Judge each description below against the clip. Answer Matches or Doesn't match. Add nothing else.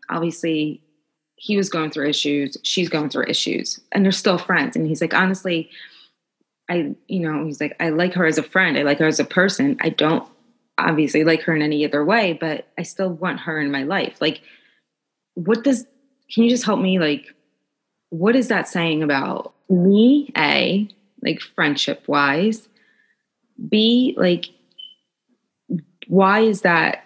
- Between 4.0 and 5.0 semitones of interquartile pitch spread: Doesn't match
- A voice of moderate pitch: Matches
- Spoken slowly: Doesn't match